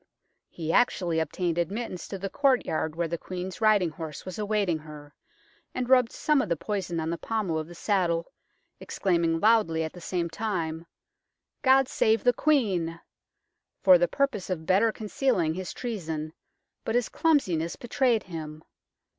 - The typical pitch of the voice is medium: Yes, medium, 180 Hz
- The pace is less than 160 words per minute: No, average, 165 wpm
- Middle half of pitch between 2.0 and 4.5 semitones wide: No, average, 5.3 semitones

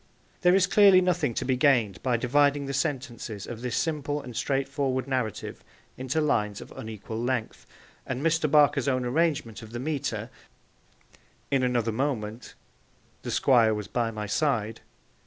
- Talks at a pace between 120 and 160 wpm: Yes, average, 155 wpm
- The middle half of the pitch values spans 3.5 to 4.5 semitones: Yes, average, 4.1 semitones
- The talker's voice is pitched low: Yes, low, 130 Hz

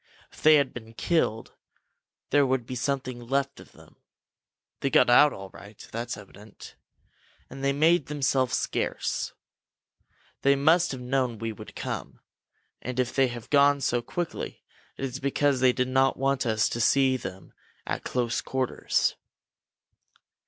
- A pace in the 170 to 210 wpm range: No, average, 150 wpm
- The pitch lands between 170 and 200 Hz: No, low, 130 Hz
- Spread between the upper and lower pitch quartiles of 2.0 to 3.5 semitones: Yes, narrow, 2.5 semitones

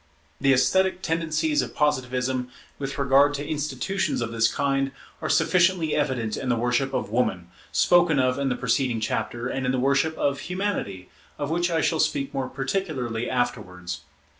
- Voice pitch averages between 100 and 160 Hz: Yes, low, 135 Hz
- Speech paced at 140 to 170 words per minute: Yes, average, 165 wpm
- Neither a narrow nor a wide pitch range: Yes, average, 4.1 semitones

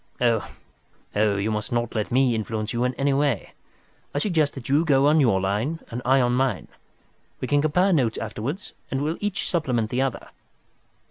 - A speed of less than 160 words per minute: No, average, 185 wpm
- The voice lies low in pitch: Yes, low, 130 Hz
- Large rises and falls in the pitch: No, average, 4.5 semitones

